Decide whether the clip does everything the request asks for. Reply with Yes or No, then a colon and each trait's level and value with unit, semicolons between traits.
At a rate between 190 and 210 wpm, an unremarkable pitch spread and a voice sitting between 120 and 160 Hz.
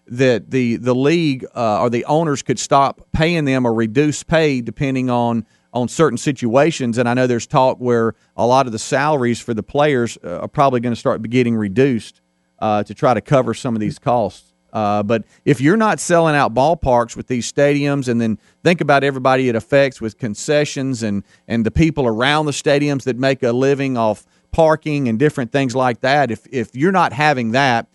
Yes: average, 200 wpm; average, 3.7 semitones; low, 130 Hz